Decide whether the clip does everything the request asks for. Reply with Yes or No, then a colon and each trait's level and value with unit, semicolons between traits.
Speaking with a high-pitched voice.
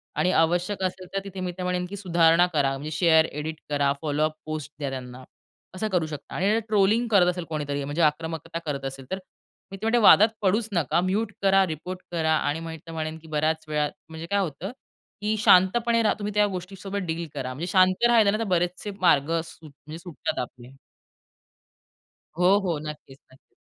No: medium, 170 Hz